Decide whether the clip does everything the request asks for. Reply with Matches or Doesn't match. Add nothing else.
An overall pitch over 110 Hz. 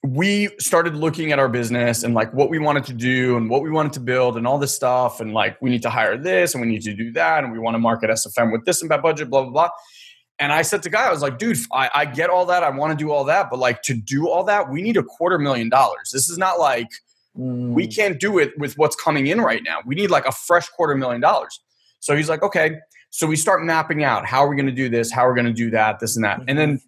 Matches